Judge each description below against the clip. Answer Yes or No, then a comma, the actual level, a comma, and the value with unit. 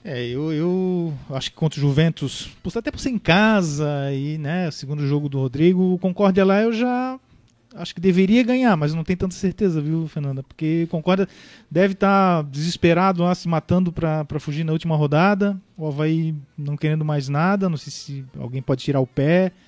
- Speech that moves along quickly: Yes, fast, 195 wpm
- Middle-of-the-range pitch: Yes, medium, 165 Hz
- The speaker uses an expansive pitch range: No, average, 4.3 semitones